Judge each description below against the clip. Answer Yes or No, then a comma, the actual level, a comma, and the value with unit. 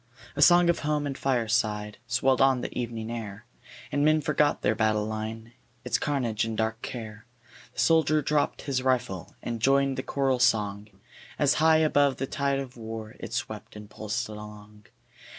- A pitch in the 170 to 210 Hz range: No, low, 120 Hz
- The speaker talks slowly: No, average, 170 wpm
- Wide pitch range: No, average, 4.2 semitones